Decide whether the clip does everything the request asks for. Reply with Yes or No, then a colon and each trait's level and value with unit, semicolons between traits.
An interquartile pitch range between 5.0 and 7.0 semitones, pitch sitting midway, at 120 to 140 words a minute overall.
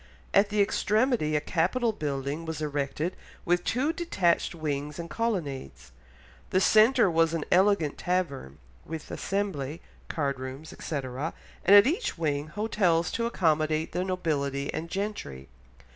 Yes: wide, 5.6 semitones; medium, 165 Hz; slow, 135 wpm